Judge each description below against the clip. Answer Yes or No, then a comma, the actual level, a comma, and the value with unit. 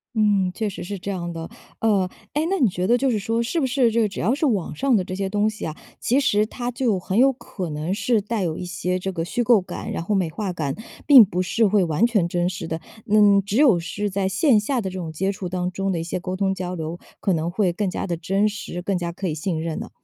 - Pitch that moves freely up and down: No, average, 3.7 semitones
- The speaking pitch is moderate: No, high, 195 Hz